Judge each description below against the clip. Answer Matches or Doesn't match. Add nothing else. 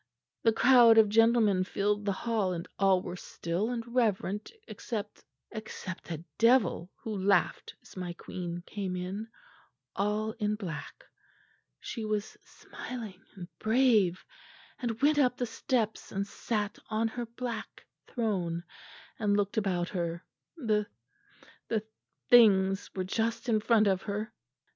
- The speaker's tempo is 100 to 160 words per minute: Matches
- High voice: Matches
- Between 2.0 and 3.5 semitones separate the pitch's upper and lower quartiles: Matches